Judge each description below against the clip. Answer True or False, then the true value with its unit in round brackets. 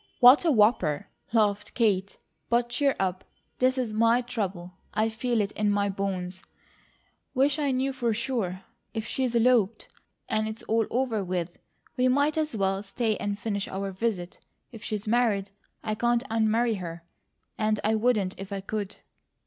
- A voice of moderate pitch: False (220 Hz)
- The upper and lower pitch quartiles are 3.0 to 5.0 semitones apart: True (3.5 semitones)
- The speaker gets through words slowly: False (165 wpm)